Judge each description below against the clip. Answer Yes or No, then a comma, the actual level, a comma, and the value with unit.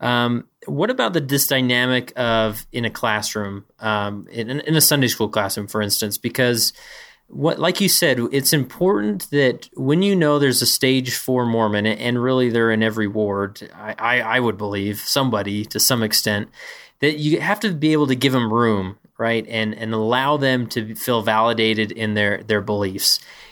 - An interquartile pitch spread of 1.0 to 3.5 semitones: No, average, 3.9 semitones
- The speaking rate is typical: Yes, average, 185 wpm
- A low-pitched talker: Yes, low, 115 Hz